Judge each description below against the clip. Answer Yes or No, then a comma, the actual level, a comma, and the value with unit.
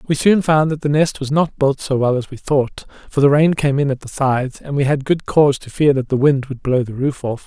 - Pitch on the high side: No, medium, 140 Hz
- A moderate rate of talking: No, fast, 295 wpm